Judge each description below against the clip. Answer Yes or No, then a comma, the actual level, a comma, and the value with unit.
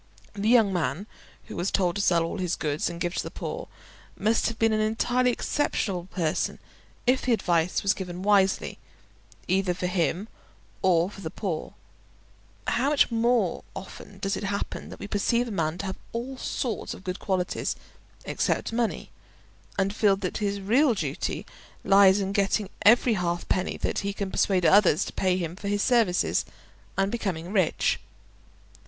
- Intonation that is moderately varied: Yes, average, 3.3 semitones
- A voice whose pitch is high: Yes, high, 195 Hz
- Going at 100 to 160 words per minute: No, average, 170 wpm